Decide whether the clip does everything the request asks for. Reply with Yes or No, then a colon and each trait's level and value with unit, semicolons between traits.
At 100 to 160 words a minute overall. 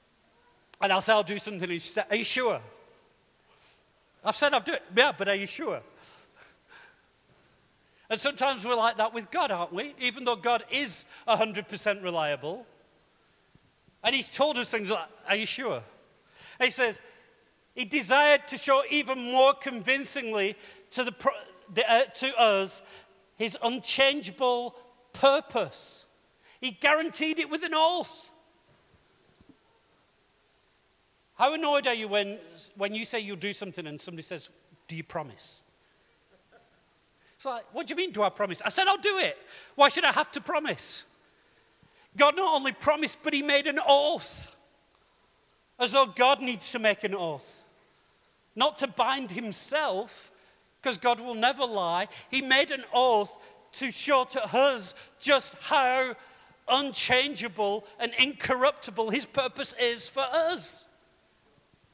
Yes: average, 145 wpm